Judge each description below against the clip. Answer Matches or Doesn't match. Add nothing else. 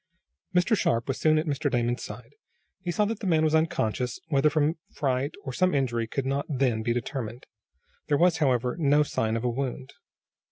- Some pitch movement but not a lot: Matches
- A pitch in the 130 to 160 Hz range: Matches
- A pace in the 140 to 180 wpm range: Doesn't match